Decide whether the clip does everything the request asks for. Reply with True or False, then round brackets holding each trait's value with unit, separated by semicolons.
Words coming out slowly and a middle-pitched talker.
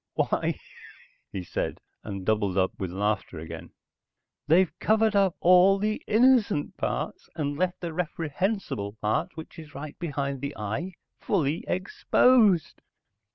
True (130 wpm; 160 Hz)